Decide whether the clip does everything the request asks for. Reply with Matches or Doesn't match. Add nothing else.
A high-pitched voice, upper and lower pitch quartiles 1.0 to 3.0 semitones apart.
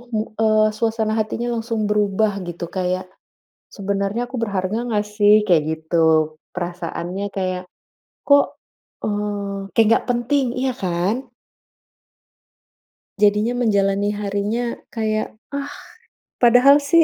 Matches